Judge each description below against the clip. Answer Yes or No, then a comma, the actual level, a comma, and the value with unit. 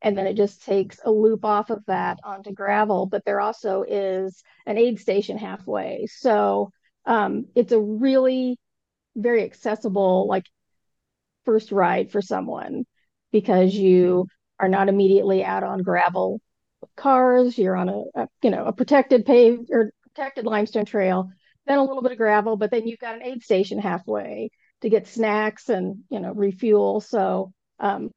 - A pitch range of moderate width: Yes, average, 3.2 semitones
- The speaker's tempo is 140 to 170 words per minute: Yes, average, 165 wpm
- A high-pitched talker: Yes, high, 210 Hz